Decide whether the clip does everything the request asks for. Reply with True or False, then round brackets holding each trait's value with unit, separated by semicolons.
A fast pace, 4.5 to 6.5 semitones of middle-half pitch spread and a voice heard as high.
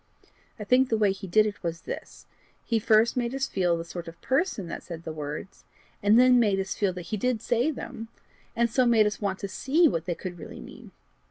True (235 wpm; 5.0 semitones; 210 Hz)